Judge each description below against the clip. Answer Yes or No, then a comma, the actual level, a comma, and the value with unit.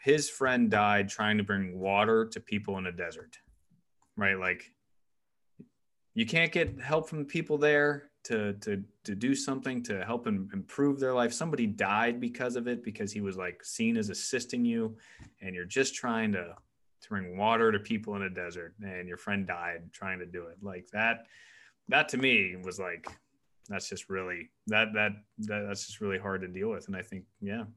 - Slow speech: No, average, 195 wpm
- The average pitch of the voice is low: Yes, low, 105 Hz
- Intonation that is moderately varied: No, wide, 5.7 semitones